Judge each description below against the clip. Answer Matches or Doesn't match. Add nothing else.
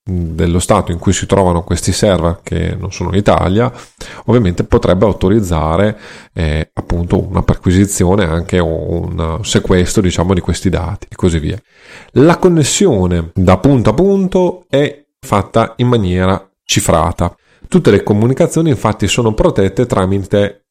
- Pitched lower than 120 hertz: Matches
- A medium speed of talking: Matches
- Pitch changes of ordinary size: Matches